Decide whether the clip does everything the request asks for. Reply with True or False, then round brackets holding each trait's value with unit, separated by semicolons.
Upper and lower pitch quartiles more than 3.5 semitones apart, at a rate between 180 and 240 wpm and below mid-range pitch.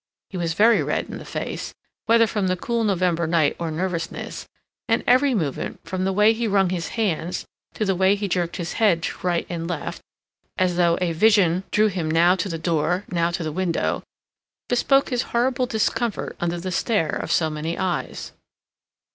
False (4.0 semitones; 190 wpm; 185 Hz)